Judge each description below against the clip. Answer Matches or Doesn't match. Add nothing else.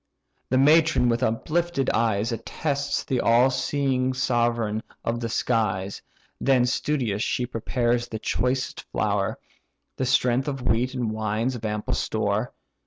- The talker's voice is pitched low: Matches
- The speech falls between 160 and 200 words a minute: Doesn't match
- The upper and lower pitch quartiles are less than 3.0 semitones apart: Matches